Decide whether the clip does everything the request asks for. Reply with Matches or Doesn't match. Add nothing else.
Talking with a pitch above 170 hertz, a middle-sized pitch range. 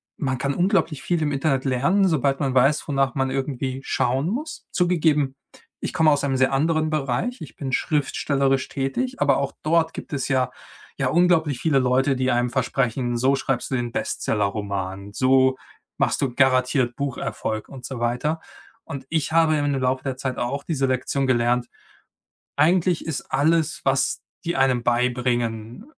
Doesn't match